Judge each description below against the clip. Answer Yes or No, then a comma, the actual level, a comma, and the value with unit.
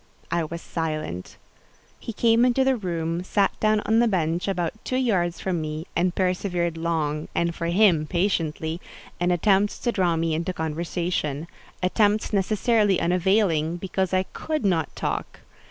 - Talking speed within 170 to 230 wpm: No, average, 150 wpm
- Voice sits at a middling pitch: Yes, medium, 175 Hz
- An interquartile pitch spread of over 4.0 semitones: No, average, 3.7 semitones